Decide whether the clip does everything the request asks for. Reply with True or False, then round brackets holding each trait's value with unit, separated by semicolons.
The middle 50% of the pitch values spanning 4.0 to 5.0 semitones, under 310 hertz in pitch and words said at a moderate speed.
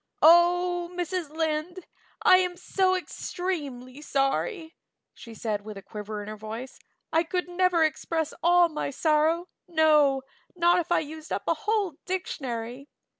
False (4.6 semitones; 320 Hz; 145 wpm)